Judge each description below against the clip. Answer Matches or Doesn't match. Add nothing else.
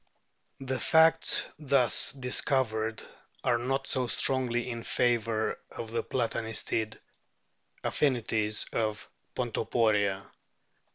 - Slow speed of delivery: Matches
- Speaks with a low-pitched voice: Matches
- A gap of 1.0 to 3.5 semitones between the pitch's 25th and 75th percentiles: Matches